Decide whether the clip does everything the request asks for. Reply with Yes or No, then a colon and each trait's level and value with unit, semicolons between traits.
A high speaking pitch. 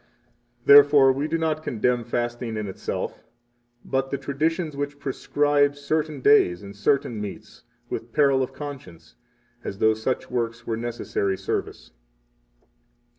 No: low, 135 Hz